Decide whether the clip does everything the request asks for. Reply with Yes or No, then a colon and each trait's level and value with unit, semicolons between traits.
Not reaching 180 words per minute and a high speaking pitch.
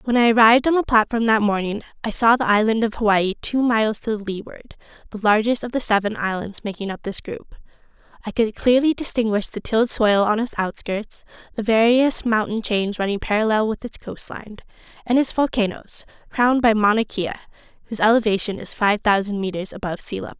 No: average, 185 wpm; high, 220 Hz